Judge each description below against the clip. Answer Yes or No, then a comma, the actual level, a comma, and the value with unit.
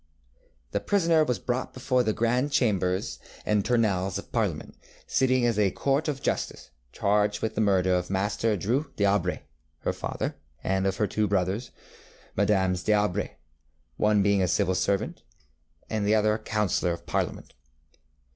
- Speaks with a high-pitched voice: No, low, 105 Hz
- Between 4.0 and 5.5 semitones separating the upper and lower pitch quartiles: No, average, 3.5 semitones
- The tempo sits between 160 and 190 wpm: No, average, 150 wpm